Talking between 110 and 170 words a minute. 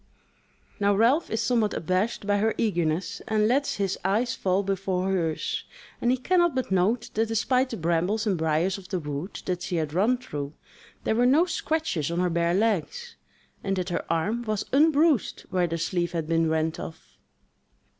No: average, 185 wpm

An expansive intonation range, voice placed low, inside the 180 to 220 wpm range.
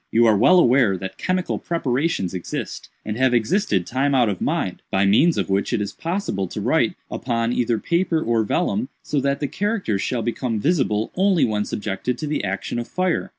Yes: wide, 8.0 semitones; low, 120 Hz; average, 195 wpm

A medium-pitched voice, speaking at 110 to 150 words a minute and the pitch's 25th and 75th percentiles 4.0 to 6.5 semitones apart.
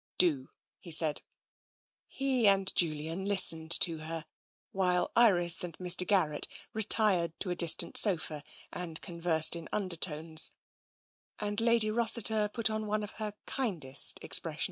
Yes: medium, 180 Hz; average, 145 wpm; average, 4.5 semitones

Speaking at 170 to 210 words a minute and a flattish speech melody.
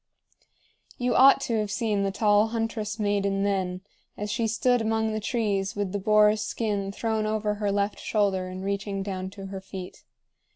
Yes: average, 175 wpm; narrow, 2.0 semitones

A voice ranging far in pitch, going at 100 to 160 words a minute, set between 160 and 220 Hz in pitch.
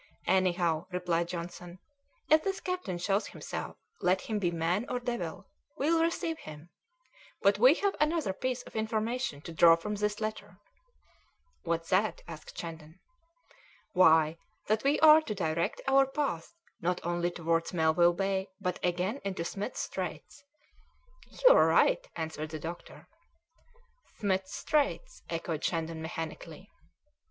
Yes: wide, 6.3 semitones; slow, 135 wpm; medium, 185 Hz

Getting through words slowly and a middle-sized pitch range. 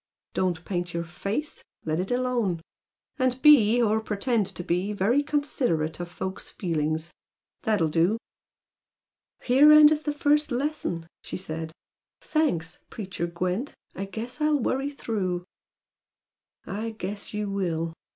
No: slow, 130 wpm; wide, 6.5 semitones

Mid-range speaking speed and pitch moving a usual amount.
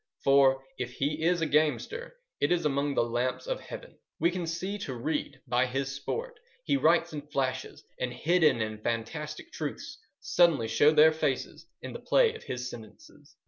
Yes: average, 180 wpm; average, 5.0 semitones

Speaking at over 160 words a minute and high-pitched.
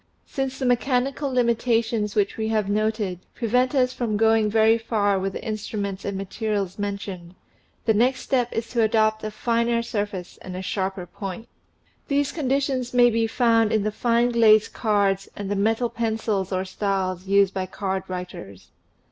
Yes: average, 170 wpm; high, 220 Hz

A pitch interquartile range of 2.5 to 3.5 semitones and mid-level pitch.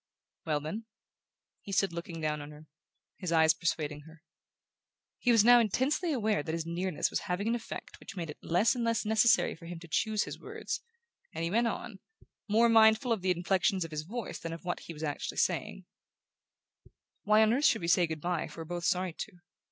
No: average, 5.1 semitones; medium, 180 Hz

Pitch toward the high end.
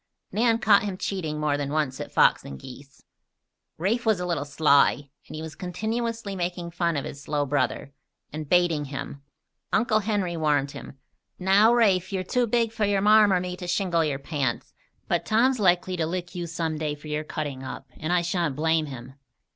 No: medium, 170 Hz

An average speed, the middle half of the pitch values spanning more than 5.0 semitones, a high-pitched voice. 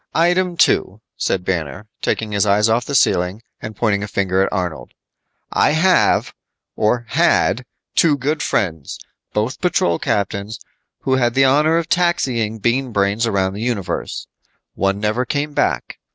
No: average, 150 wpm; wide, 5.4 semitones; low, 110 Hz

